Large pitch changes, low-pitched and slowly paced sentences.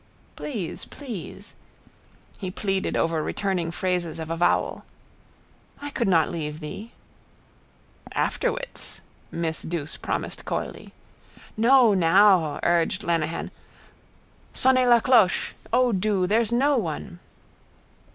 No: wide, 5.8 semitones; high, 190 Hz; slow, 100 wpm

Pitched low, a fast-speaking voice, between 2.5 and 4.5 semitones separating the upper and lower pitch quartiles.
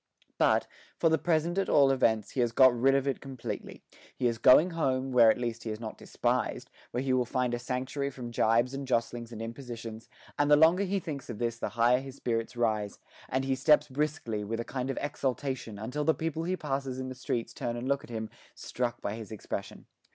Yes: low, 125 Hz; fast, 225 wpm; average, 3.1 semitones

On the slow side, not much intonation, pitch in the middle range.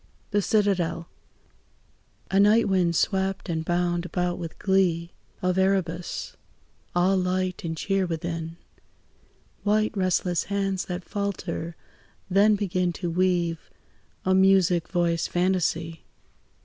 Yes: slow, 110 wpm; narrow, 2.1 semitones; medium, 180 Hz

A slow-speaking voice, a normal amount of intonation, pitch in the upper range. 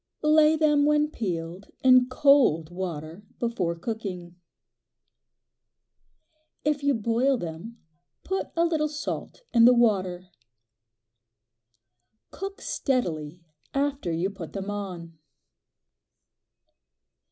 No: slow, 95 wpm; wide, 8.3 semitones; high, 225 Hz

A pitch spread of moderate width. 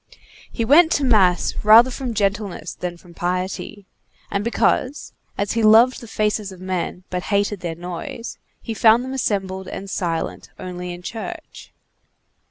Yes: average, 4.1 semitones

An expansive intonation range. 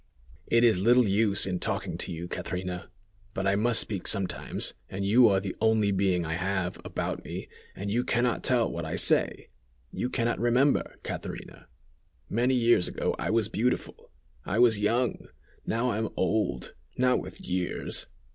No: average, 4.0 semitones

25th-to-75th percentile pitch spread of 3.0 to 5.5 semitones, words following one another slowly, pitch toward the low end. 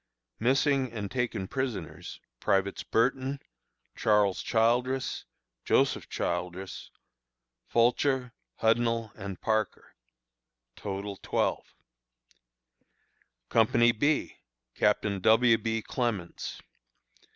Yes: average, 3.6 semitones; slow, 75 wpm; low, 115 Hz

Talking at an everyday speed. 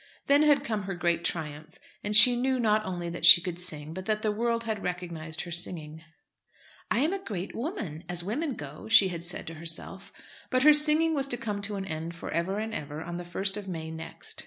No: fast, 230 wpm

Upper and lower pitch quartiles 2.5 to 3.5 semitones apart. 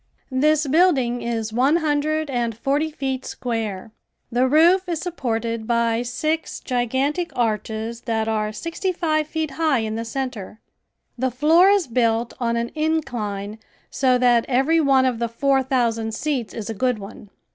No: average, 5.0 semitones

